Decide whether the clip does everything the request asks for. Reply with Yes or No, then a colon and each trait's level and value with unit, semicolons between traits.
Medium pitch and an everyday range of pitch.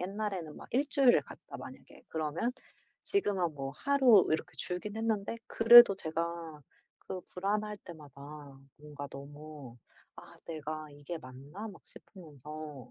No: medium, 170 Hz; wide, 5.9 semitones